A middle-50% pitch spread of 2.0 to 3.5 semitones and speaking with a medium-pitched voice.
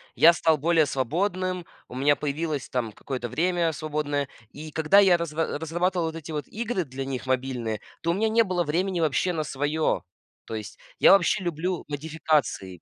No: average, 3.9 semitones; medium, 155 Hz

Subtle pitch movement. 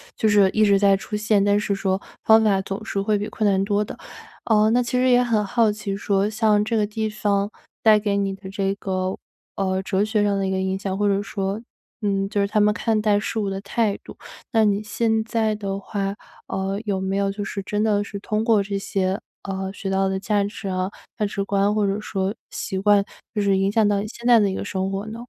Yes: narrow, 1.5 semitones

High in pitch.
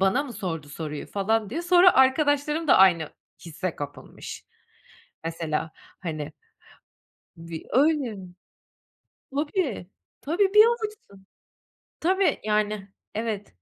Yes: high, 215 Hz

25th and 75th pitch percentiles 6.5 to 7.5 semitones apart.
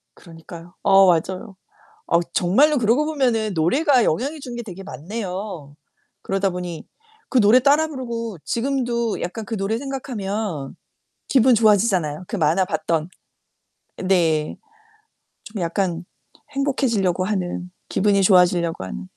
No: average, 5.2 semitones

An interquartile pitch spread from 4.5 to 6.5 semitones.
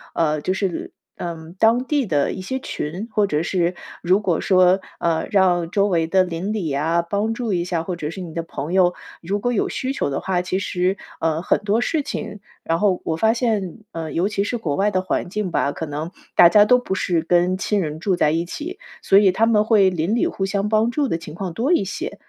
No: average, 3.9 semitones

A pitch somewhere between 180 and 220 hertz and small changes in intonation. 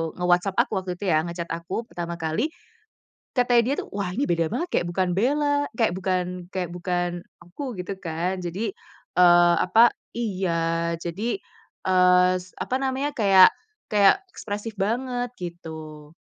No: medium, 185 Hz; average, 4.7 semitones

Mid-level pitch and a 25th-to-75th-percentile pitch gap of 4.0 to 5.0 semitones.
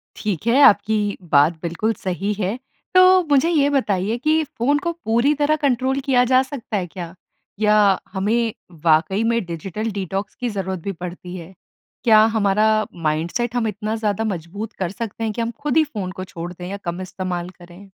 No: high, 210 Hz; average, 4.5 semitones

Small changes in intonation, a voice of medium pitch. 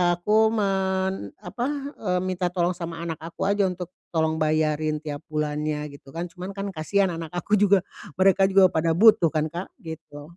No: average, 3.4 semitones; medium, 175 Hz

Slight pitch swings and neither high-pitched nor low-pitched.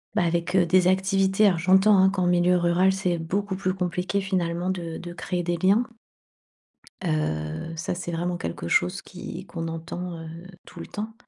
Yes: narrow, 2.0 semitones; medium, 180 Hz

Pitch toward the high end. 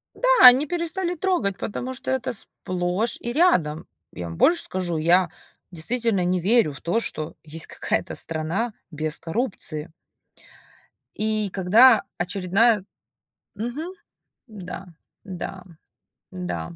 Yes: high, 195 Hz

